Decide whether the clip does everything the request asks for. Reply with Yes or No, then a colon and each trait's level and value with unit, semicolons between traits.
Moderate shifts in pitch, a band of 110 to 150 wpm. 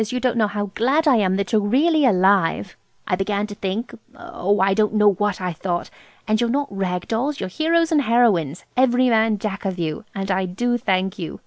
No: average, 4.3 semitones; fast, 205 wpm